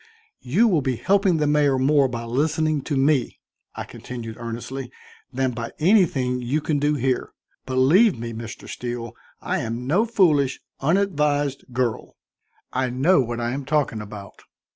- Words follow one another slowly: No, average, 155 wpm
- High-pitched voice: No, low, 135 Hz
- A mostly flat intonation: No, average, 3.9 semitones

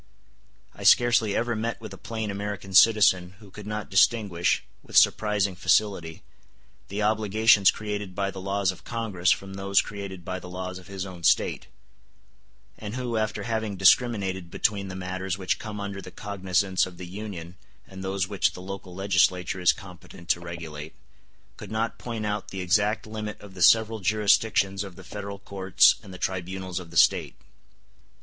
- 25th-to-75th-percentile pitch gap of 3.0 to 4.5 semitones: No, narrow, 2.4 semitones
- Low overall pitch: Yes, low, 100 Hz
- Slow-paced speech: No, average, 170 wpm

